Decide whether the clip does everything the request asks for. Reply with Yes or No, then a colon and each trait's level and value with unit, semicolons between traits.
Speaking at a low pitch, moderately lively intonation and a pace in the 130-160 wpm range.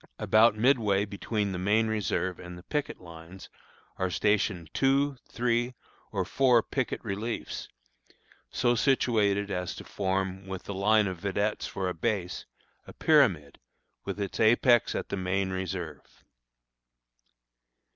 Yes: low, 100 Hz; average, 3.5 semitones; slow, 135 wpm